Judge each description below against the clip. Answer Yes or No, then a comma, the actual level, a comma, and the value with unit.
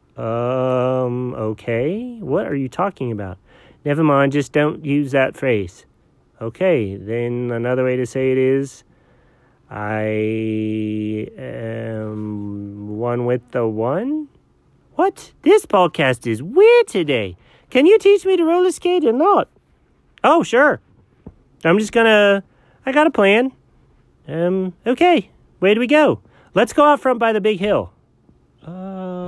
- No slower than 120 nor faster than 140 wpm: Yes, slow, 135 wpm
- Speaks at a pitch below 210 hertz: Yes, medium, 140 Hz